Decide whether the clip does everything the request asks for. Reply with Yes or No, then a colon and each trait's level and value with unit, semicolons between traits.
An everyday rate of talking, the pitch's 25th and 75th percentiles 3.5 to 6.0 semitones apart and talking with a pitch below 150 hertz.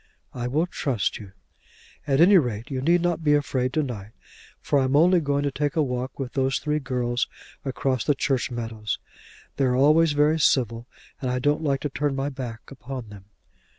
No: average, 195 wpm; average, 3.1 semitones; low, 135 Hz